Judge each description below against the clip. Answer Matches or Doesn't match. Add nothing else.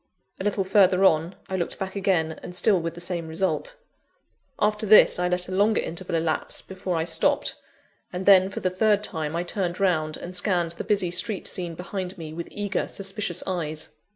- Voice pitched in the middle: Matches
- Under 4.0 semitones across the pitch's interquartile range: Matches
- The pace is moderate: Matches